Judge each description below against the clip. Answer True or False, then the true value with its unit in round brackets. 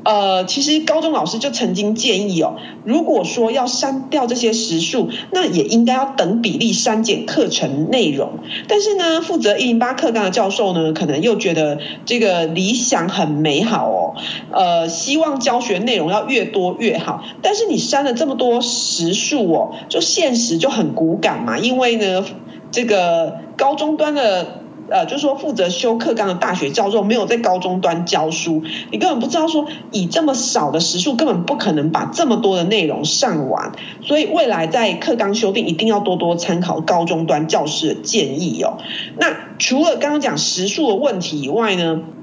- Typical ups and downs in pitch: False (7.2 semitones)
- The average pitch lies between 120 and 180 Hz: False (225 Hz)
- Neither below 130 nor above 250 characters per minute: False (275 characters per minute)